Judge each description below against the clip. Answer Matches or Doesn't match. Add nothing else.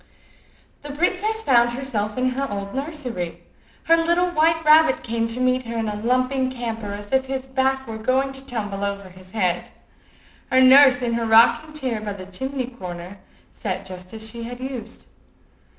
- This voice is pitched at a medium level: Doesn't match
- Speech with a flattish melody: Doesn't match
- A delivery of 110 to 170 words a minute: Doesn't match